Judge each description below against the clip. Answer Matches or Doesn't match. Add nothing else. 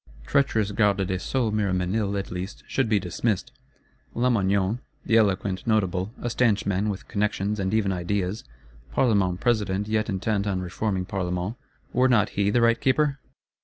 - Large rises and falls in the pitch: Doesn't match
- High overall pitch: Doesn't match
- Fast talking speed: Doesn't match